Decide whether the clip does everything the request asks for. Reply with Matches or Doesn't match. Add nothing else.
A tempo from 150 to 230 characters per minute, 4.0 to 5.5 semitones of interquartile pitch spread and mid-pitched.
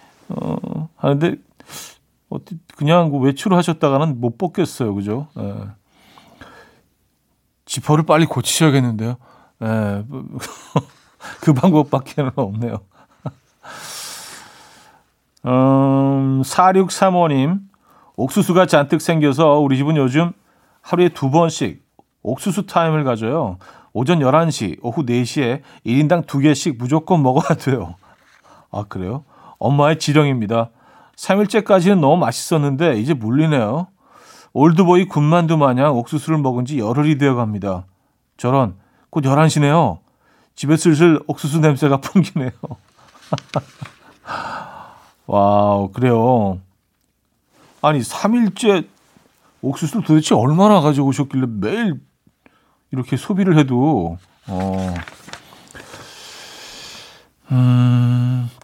Matches